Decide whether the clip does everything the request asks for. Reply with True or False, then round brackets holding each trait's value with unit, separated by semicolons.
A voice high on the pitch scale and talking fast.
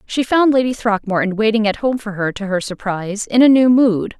True (220 Hz; 230 wpm)